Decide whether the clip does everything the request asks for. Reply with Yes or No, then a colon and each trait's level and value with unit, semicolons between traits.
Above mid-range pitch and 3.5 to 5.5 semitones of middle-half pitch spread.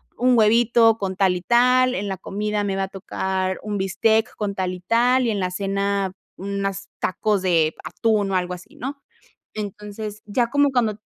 No: high, 205 Hz; average, 2.9 semitones